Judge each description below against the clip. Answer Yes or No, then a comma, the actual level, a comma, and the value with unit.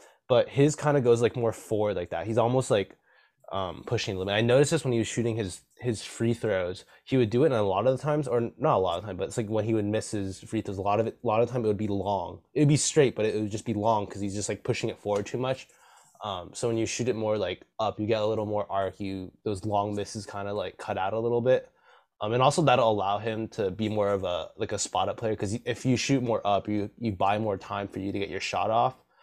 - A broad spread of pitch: No, average, 2.7 semitones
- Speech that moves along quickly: Yes, fast, 305 wpm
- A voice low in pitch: Yes, low, 110 Hz